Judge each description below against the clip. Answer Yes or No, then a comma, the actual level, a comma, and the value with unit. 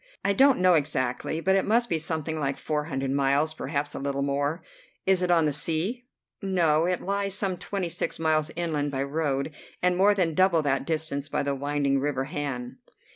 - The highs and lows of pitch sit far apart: No, average, 4.3 semitones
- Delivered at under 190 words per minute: No, average, 195 wpm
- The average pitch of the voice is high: No, medium, 155 Hz